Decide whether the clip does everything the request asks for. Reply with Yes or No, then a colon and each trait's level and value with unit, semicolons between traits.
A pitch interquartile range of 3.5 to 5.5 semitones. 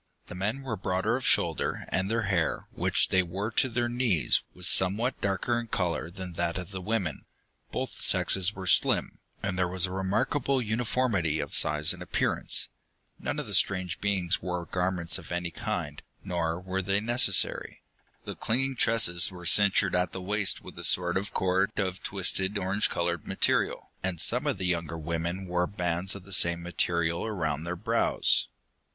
No: narrow, 2.6 semitones